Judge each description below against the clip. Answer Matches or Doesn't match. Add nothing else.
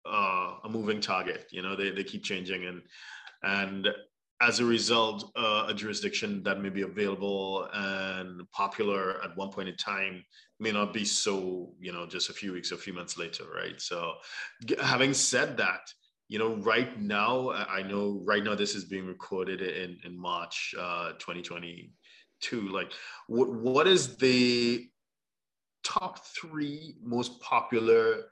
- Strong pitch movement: Doesn't match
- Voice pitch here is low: Matches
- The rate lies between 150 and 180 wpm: Matches